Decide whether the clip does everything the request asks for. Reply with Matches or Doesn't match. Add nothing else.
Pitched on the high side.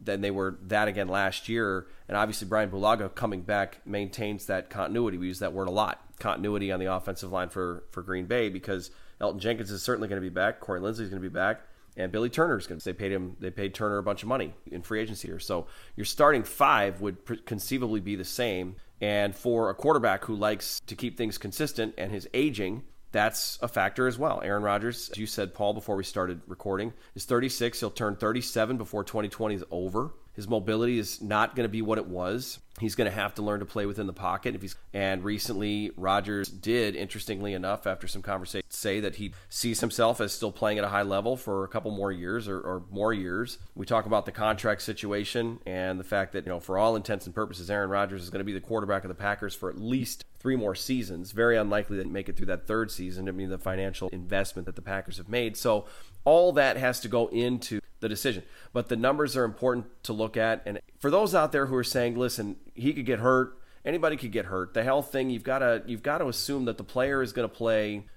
Doesn't match